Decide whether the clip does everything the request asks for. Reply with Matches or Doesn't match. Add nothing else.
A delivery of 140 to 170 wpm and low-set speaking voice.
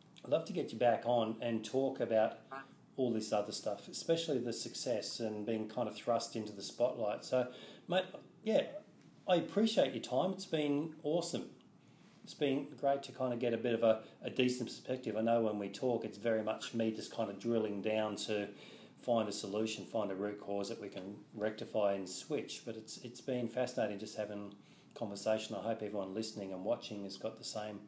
Doesn't match